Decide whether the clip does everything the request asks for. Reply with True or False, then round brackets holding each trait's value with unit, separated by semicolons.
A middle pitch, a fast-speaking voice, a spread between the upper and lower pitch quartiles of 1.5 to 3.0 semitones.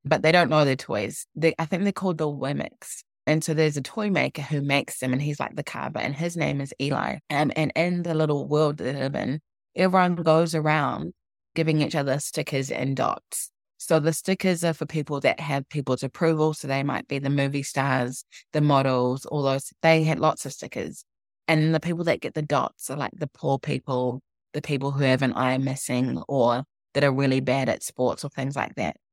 True (145 Hz; 220 wpm; 2.7 semitones)